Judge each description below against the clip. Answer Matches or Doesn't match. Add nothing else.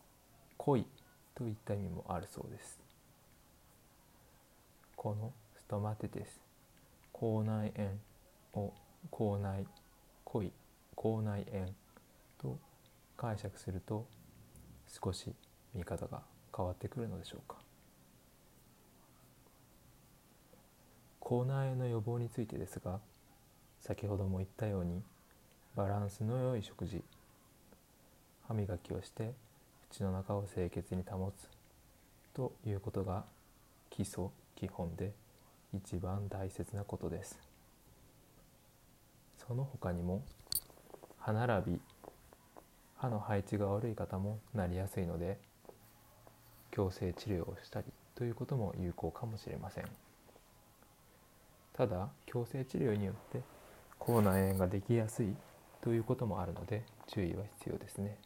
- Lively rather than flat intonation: Doesn't match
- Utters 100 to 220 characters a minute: Matches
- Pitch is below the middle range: Matches